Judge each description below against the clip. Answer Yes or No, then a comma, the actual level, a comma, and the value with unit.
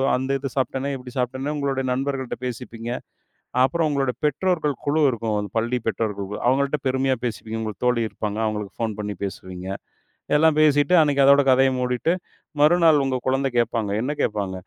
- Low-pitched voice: Yes, low, 130 Hz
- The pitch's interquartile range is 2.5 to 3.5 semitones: No, average, 4.0 semitones